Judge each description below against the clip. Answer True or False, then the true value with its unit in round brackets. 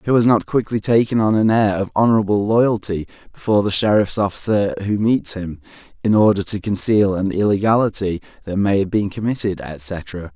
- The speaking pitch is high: False (100 Hz)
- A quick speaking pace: False (175 wpm)